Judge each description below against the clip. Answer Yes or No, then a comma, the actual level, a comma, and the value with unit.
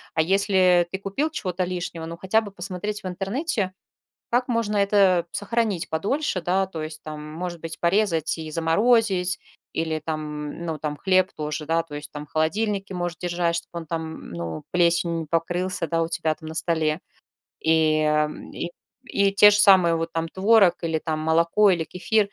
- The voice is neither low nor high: Yes, medium, 175 Hz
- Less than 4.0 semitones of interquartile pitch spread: Yes, average, 3.5 semitones